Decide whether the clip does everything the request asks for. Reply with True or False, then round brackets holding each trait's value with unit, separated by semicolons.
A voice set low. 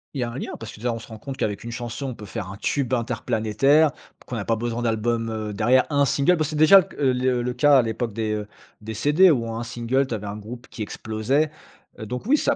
True (120 Hz)